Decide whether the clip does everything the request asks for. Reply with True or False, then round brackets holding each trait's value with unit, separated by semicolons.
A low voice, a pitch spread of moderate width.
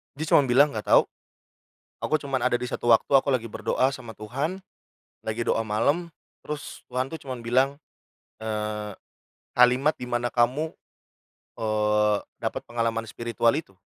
True (120 Hz; 3.5 semitones)